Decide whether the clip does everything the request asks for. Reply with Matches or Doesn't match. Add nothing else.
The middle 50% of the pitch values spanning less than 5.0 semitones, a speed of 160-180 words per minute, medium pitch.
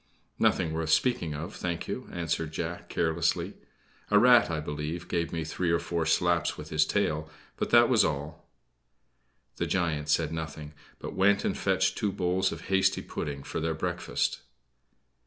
Doesn't match